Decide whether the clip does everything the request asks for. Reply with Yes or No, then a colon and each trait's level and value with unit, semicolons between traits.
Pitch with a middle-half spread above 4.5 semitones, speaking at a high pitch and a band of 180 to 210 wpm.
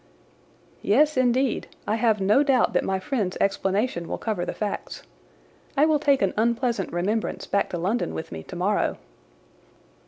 No: average, 5.0 semitones; high, 220 Hz; average, 155 wpm